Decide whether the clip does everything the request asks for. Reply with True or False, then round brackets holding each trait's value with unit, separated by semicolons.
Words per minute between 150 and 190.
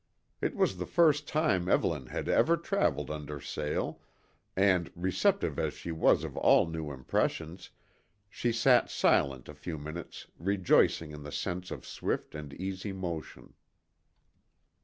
False (140 wpm)